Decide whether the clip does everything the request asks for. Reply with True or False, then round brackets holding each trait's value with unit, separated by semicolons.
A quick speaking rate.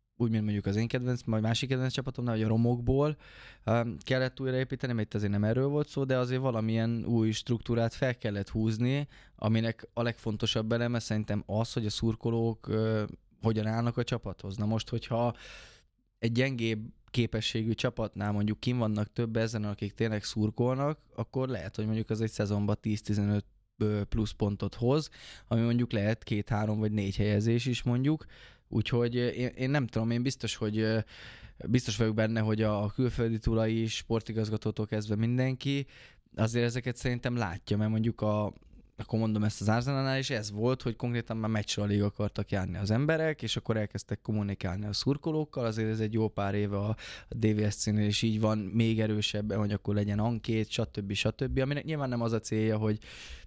True (170 wpm)